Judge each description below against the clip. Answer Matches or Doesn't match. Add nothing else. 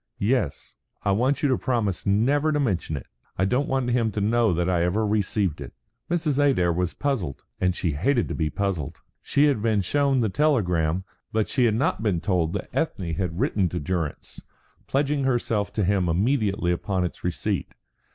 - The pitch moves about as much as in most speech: Doesn't match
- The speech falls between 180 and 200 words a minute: Matches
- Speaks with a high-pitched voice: Doesn't match